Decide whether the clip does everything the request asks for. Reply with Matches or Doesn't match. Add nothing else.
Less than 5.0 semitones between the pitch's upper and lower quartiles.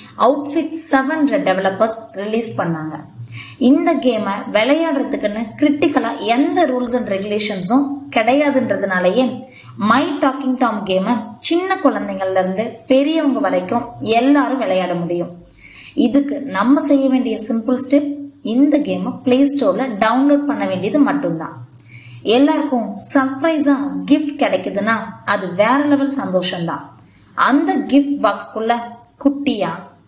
Doesn't match